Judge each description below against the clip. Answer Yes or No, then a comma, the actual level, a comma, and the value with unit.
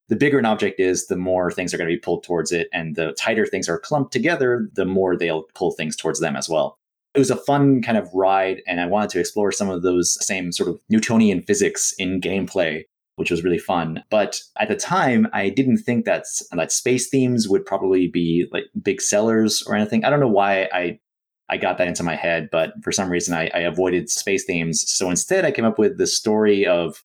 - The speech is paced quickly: Yes, fast, 235 wpm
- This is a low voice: Yes, very low, 95 Hz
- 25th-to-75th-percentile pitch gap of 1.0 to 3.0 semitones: No, average, 4.2 semitones